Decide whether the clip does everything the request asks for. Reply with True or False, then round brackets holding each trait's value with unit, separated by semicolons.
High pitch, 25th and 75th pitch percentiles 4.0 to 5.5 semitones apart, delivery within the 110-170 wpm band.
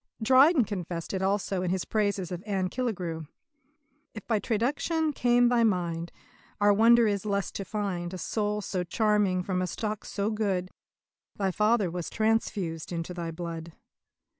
False (200 Hz; 3.5 semitones; 165 wpm)